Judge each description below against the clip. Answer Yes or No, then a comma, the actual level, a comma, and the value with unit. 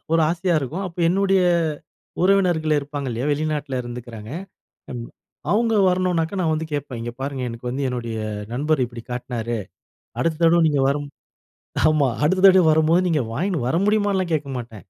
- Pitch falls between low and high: Yes, medium, 155 Hz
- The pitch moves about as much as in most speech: No, wide, 6.0 semitones